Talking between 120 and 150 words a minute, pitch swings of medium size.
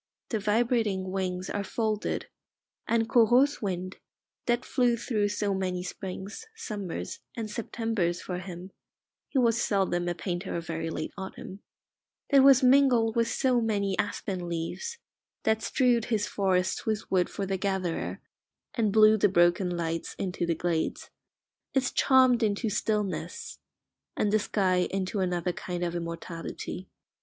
Yes: average, 145 wpm; average, 3.9 semitones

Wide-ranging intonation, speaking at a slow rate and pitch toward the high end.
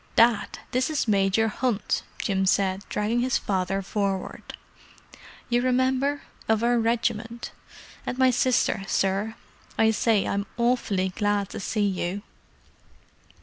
No: average, 3.6 semitones; slow, 125 wpm; high, 220 Hz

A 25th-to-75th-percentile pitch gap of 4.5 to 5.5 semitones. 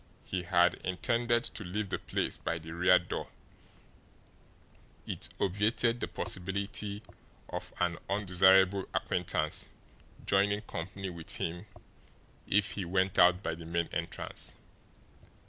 No: narrow, 2.6 semitones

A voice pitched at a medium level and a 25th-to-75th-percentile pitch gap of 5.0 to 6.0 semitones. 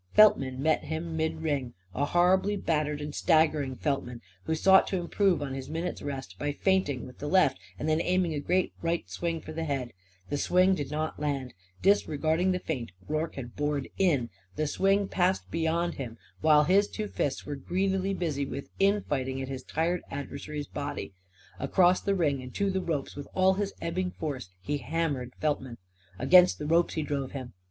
No: medium, 155 Hz; average, 4.3 semitones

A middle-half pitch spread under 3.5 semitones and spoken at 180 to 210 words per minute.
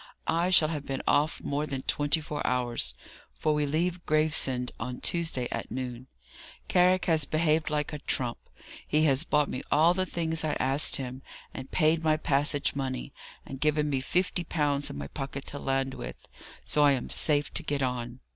Yes: average, 2.9 semitones; average, 185 wpm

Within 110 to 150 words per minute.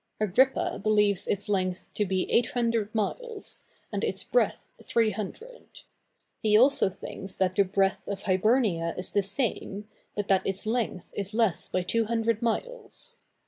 Yes: average, 140 wpm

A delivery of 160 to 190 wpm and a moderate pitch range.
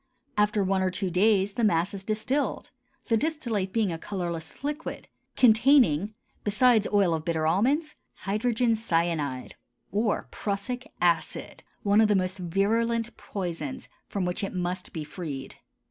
No: average, 145 wpm; average, 4.4 semitones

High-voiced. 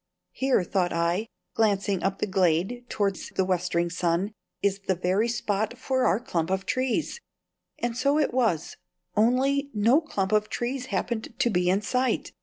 Yes: high, 210 Hz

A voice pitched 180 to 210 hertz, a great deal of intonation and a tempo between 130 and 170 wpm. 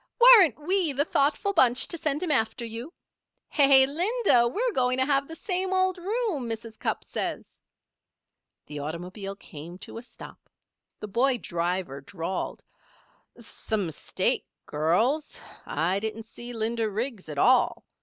No: high, 245 Hz; wide, 7.4 semitones; average, 145 wpm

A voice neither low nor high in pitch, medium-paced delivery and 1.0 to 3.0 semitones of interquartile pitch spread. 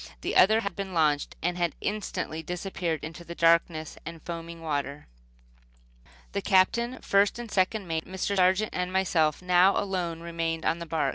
Yes: medium, 175 Hz; average, 165 wpm; average, 2.7 semitones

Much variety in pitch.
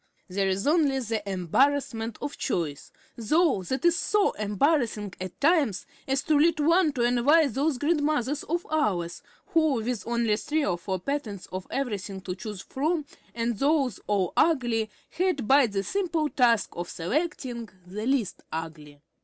Yes: wide, 6.9 semitones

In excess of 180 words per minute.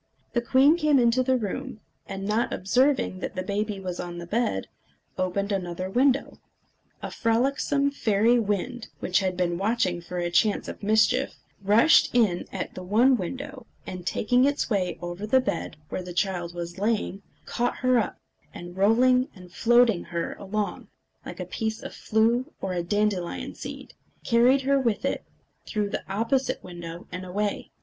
No: average, 170 wpm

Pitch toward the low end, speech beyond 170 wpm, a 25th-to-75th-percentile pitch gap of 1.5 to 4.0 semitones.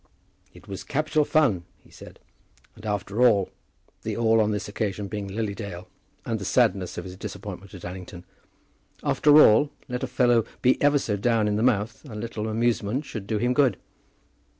Yes: low, 110 Hz; average, 180 wpm; average, 3.4 semitones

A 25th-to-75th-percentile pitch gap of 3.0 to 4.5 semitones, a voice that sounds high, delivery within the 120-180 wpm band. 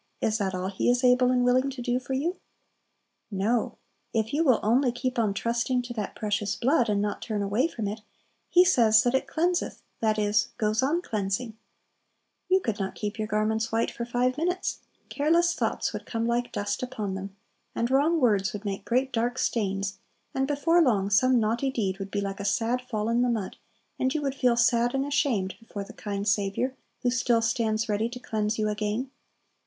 No: average, 3.5 semitones; high, 230 Hz; average, 200 wpm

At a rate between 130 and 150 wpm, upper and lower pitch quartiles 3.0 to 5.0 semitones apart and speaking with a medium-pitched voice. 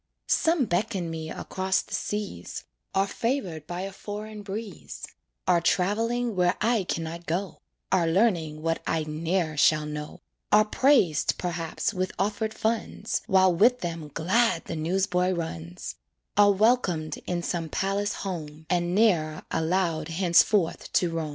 Yes: average, 145 wpm; average, 4.0 semitones; medium, 180 Hz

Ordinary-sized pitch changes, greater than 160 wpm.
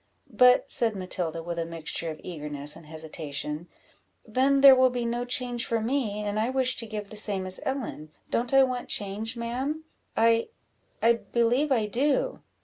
No: wide, 5.7 semitones; average, 175 wpm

